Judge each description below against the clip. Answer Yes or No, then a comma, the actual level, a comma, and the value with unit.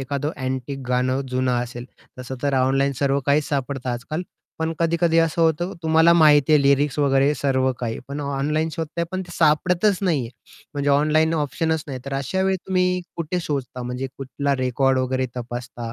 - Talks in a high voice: No, medium, 140 Hz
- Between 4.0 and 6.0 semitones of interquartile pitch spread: No, average, 3.5 semitones